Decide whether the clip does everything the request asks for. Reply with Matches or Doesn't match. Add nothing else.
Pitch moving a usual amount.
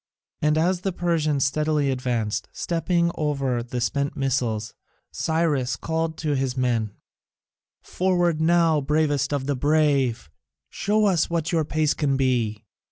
Matches